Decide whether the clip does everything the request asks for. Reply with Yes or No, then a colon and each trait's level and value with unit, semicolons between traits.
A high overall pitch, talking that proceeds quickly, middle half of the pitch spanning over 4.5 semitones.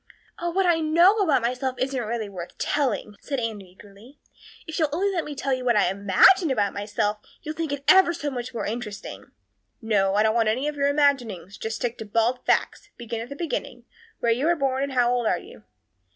Yes: very high, 250 Hz; fast, 225 wpm; average, 5.3 semitones